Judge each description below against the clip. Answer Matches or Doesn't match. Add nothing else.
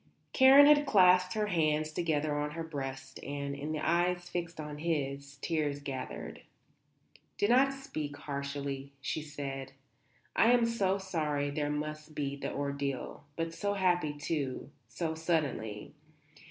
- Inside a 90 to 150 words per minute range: Matches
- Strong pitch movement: Doesn't match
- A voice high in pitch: Doesn't match